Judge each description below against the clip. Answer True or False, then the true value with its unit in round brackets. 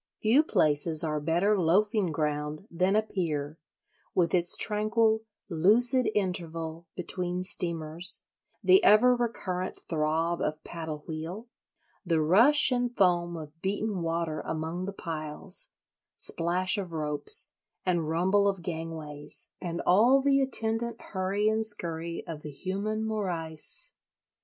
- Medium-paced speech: False (125 wpm)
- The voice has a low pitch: False (180 Hz)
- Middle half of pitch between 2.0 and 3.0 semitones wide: False (4.6 semitones)